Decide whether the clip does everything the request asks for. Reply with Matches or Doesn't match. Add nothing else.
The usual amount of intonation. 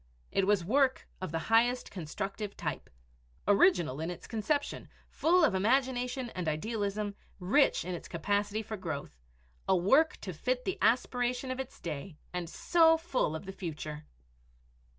Doesn't match